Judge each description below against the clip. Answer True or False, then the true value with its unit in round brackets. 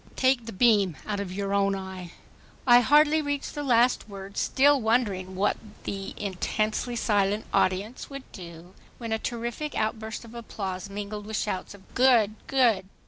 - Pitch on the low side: False (215 Hz)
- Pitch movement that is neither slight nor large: True (3.7 semitones)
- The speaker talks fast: False (160 wpm)